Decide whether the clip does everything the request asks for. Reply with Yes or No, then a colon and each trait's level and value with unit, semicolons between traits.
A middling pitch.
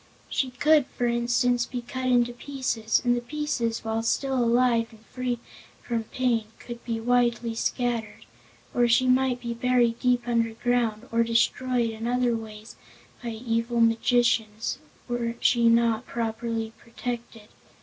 No: high, 240 Hz